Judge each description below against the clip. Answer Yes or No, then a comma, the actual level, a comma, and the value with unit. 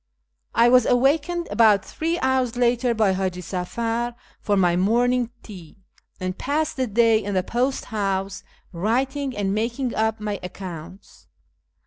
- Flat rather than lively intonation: No, average, 4.4 semitones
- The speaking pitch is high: Yes, high, 225 Hz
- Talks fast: No, average, 140 wpm